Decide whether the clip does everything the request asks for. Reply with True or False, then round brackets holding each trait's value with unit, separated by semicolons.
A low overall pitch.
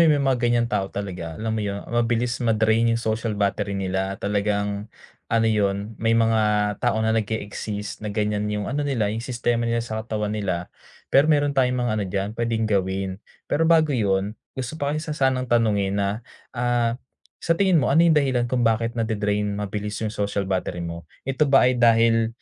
True (110 Hz)